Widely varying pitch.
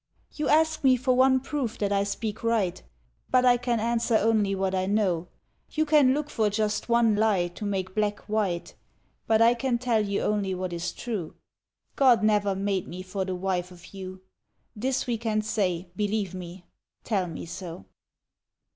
No: average, 4.0 semitones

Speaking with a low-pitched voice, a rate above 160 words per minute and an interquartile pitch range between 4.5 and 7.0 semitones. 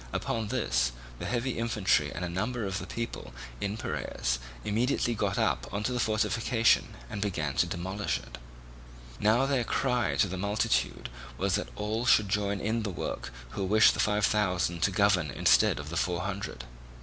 No: low, 100 Hz; average, 175 wpm; average, 3.9 semitones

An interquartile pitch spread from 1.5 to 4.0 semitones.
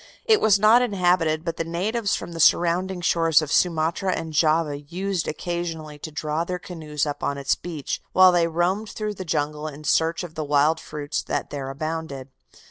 Yes: average, 2.9 semitones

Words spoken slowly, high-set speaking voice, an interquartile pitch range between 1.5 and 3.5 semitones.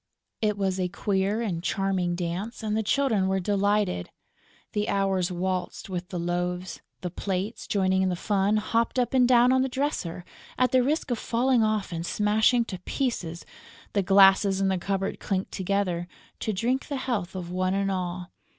No: average, 180 wpm; high, 195 Hz; average, 3.2 semitones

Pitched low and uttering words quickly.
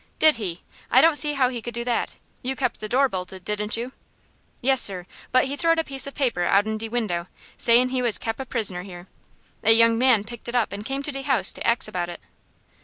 No: high, 235 Hz; fast, 240 wpm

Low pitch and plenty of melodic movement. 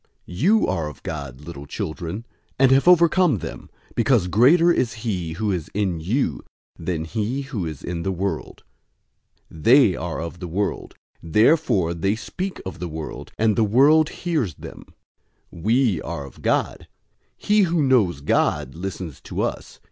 Yes: low, 100 Hz; wide, 8.0 semitones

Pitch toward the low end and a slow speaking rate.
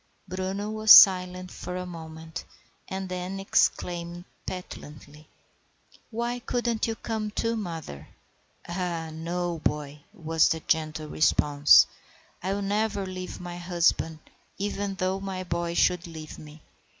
No: medium, 180 Hz; slow, 125 wpm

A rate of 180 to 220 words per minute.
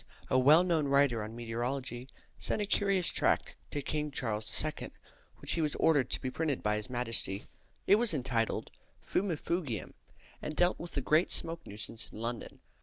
No: average, 170 wpm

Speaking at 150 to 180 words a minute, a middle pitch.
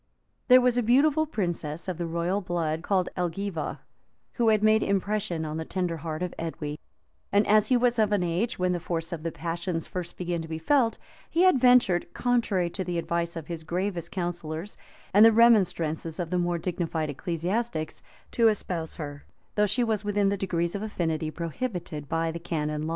No: average, 195 wpm; medium, 175 Hz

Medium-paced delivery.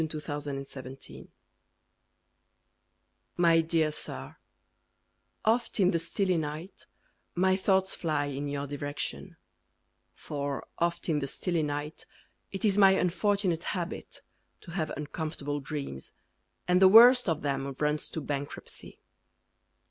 No: slow, 125 wpm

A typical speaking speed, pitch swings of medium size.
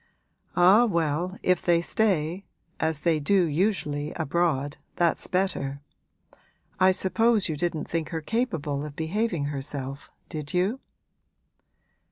No: slow, 120 wpm; average, 4.0 semitones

